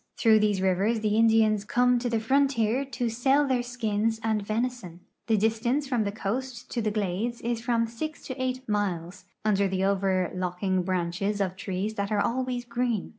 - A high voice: Yes, high, 220 Hz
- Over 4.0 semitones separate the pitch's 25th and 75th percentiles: No, average, 3.5 semitones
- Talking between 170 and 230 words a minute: Yes, average, 175 wpm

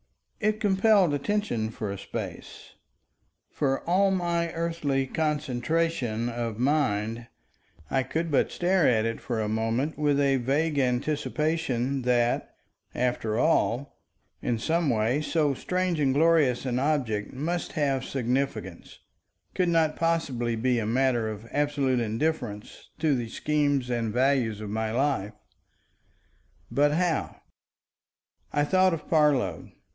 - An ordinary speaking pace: No, slow, 130 wpm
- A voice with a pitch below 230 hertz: Yes, low, 135 Hz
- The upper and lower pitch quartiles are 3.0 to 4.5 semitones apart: No, average, 5.2 semitones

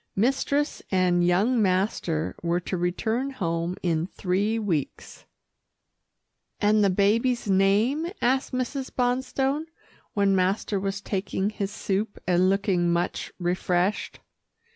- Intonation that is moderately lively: Yes, average, 4.3 semitones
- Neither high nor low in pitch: No, high, 195 Hz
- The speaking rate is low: Yes, slow, 115 wpm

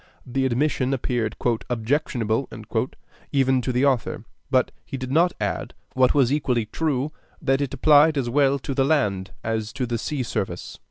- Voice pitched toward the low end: Yes, low, 130 Hz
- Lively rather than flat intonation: No, average, 2.9 semitones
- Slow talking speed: No, average, 165 wpm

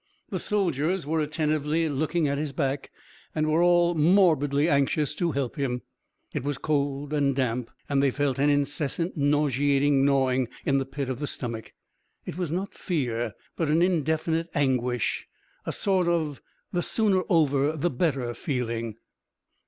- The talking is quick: No, average, 155 wpm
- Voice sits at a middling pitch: Yes, medium, 145 Hz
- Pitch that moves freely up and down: No, average, 3.0 semitones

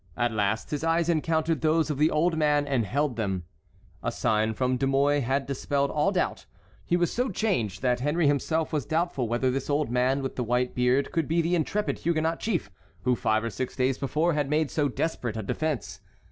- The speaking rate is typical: No, fast, 210 wpm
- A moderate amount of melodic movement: Yes, average, 4.4 semitones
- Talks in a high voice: No, medium, 145 Hz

